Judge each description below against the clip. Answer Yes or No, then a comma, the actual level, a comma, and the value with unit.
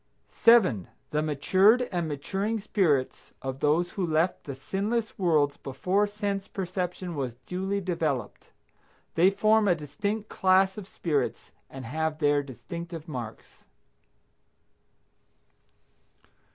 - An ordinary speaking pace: No, slow, 110 wpm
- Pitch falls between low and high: Yes, medium, 175 Hz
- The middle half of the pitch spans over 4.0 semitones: Yes, average, 5.1 semitones